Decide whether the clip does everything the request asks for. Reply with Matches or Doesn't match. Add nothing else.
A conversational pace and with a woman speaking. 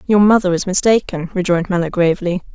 Matches